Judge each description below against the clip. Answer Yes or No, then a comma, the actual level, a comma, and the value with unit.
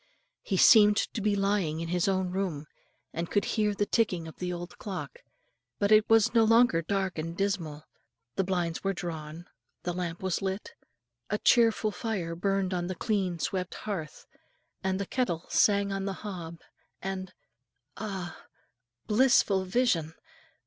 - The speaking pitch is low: No, high, 190 Hz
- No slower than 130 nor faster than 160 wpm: Yes, average, 155 wpm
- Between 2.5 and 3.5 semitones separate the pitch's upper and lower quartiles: Yes, average, 2.9 semitones